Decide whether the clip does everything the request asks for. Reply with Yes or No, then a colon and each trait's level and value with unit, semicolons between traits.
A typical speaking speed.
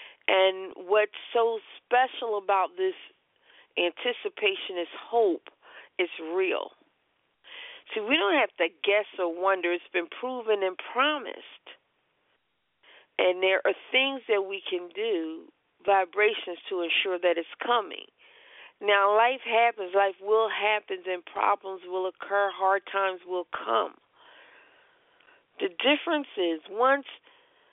No: slow, 120 wpm